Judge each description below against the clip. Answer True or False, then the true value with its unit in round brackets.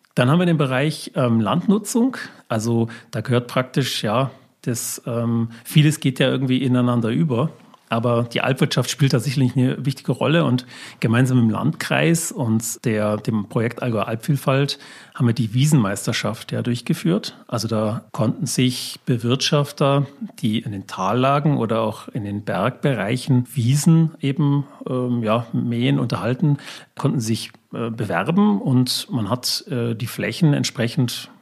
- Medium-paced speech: True (145 wpm)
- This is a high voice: False (125 Hz)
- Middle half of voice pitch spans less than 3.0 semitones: False (3.5 semitones)